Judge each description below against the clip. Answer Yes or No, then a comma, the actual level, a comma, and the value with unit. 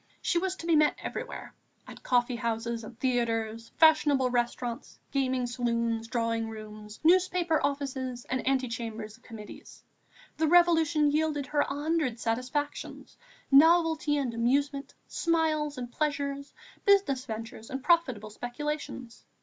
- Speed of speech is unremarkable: No, slow, 130 wpm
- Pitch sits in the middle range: No, very high, 260 Hz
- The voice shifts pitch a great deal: No, average, 4.6 semitones